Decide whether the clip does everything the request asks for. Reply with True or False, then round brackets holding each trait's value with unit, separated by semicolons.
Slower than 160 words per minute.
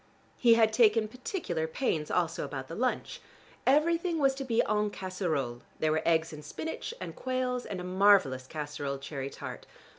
False (170 wpm)